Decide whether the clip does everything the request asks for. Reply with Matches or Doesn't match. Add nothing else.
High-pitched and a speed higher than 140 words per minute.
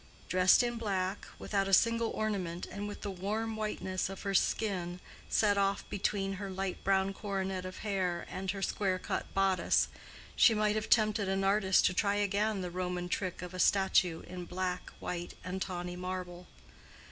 Matches